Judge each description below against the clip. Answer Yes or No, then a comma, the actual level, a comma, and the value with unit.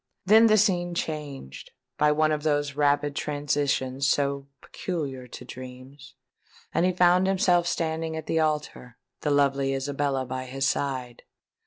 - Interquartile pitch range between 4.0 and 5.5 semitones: No, average, 3.0 semitones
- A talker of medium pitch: Yes, medium, 145 Hz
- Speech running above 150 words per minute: No, average, 145 wpm